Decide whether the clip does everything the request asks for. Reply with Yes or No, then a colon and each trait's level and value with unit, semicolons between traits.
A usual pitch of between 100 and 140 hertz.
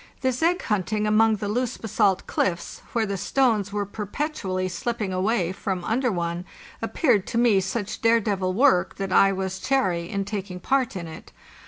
No: high, 205 Hz